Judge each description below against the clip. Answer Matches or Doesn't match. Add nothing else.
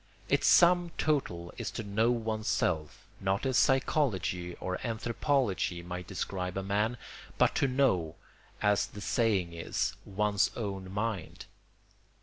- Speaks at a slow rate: Matches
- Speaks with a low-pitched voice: Matches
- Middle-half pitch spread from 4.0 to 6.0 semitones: Matches